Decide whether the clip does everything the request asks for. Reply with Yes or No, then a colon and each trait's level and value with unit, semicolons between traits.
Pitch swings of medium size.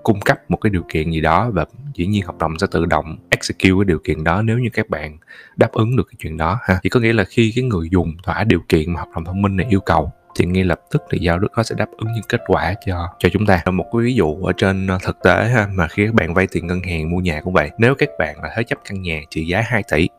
Yes: average, 4.7 semitones